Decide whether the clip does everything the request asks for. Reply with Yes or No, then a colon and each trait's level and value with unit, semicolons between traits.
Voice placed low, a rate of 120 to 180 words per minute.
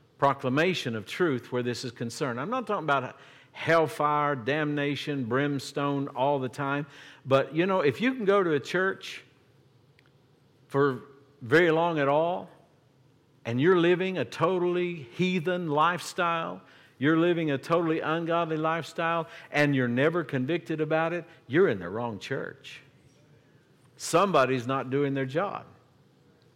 No: medium, 145 Hz; average, 140 wpm